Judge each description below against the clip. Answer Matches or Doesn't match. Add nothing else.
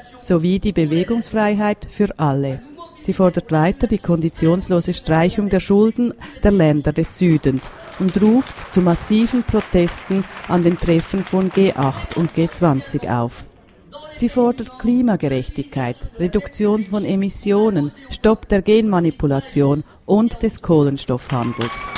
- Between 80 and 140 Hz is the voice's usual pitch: Doesn't match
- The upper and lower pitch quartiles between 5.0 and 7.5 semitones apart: Matches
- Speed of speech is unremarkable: Doesn't match